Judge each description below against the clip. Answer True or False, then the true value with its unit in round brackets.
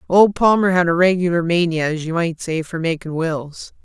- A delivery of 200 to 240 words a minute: True (205 wpm)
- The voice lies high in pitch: False (170 Hz)